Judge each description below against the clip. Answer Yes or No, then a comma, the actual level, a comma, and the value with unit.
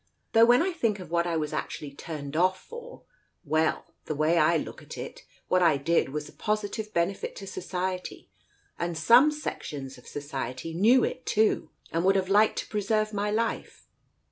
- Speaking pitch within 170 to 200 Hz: Yes, medium, 185 Hz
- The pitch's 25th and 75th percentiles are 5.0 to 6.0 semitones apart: Yes, wide, 5.5 semitones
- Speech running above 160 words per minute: Yes, average, 195 wpm